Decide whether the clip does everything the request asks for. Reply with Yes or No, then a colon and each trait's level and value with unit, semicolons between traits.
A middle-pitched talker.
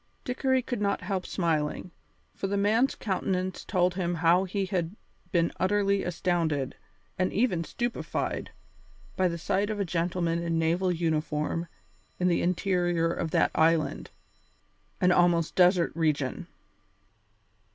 Yes: medium, 180 Hz